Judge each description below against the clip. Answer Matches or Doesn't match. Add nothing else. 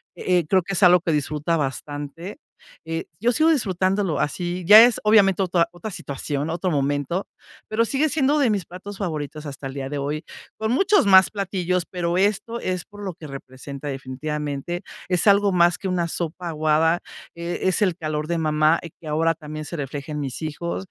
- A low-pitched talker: Doesn't match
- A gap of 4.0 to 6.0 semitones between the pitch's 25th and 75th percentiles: Matches